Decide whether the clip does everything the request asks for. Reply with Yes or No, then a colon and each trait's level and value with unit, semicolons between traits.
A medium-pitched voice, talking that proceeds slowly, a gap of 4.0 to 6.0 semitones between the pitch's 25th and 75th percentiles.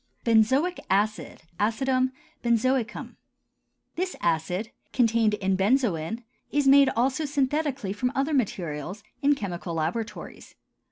No: high, 230 Hz; slow, 105 wpm; wide, 5.4 semitones